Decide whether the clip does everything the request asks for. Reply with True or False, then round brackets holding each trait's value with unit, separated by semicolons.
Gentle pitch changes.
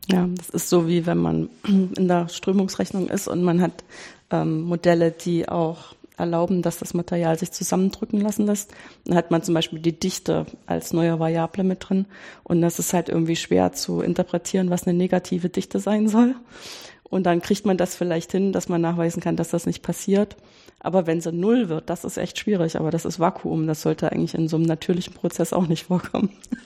True (2.2 semitones)